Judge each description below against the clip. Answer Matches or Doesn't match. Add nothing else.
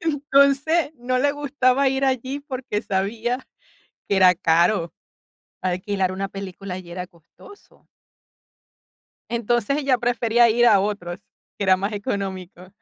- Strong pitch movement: Matches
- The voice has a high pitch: Matches